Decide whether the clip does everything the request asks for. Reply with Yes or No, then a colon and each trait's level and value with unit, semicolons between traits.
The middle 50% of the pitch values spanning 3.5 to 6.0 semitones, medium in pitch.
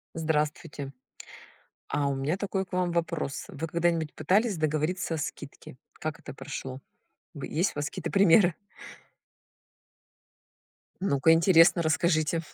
No: average, 2.9 semitones; medium, 165 Hz